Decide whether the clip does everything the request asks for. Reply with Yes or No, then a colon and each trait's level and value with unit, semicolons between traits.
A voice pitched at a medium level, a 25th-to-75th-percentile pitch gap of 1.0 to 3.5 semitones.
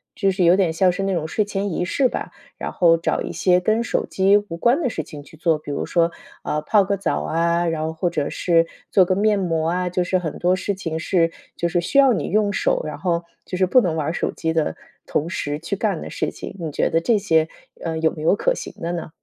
Yes: medium, 175 Hz; average, 3.2 semitones